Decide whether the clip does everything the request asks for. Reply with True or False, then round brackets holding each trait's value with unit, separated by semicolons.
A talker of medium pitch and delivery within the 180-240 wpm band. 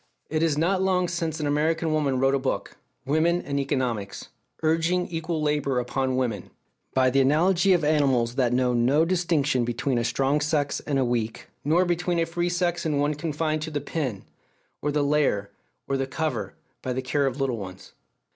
True (145 Hz; 190 wpm)